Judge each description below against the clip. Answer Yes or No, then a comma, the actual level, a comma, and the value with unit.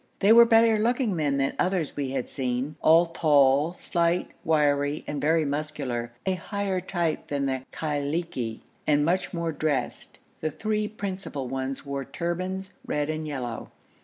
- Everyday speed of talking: Yes, average, 155 wpm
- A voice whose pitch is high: No, medium, 155 Hz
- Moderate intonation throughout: Yes, average, 4.6 semitones